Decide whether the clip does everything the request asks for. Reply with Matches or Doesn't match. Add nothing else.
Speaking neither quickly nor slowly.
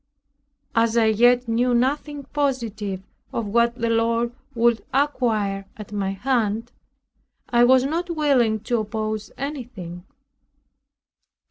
Doesn't match